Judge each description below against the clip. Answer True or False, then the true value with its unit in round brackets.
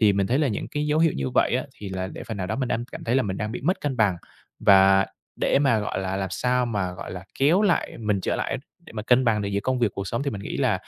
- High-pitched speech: False (110 Hz)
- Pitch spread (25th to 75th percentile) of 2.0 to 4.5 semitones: False (5.0 semitones)